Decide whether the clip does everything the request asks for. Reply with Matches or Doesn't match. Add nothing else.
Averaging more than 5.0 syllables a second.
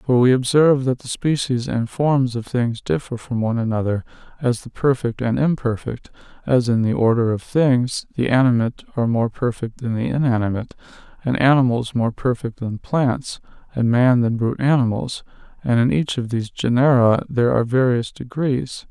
Matches